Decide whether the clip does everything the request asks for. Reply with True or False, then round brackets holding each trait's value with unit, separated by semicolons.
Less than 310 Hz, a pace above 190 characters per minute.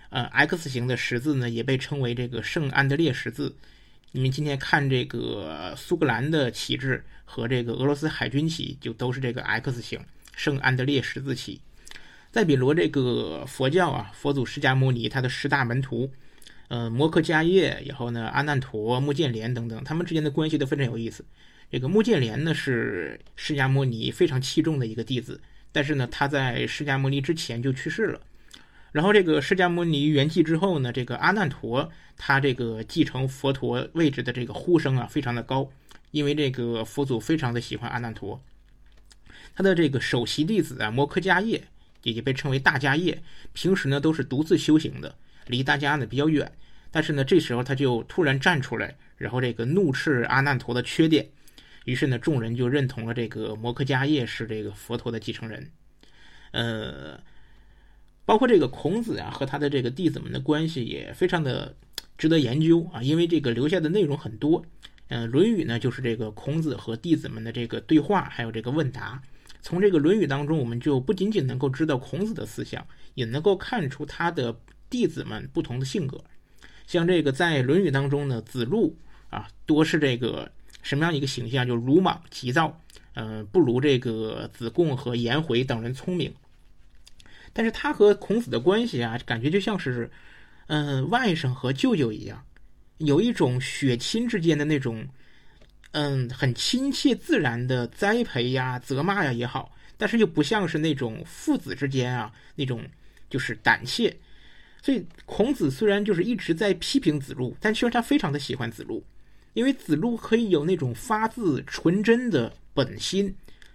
True (140 Hz; 280 characters per minute)